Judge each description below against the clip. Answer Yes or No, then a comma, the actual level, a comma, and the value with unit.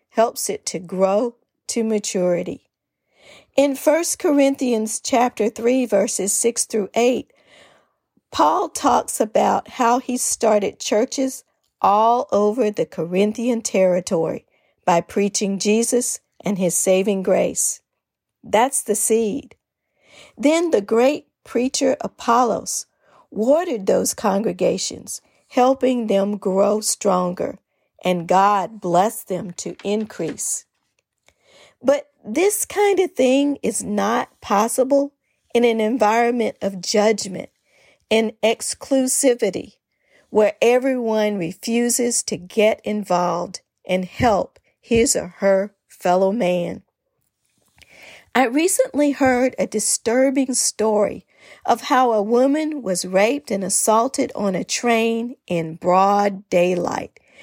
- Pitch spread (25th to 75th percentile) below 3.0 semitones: No, average, 4.3 semitones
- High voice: Yes, high, 220 Hz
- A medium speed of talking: No, slow, 110 wpm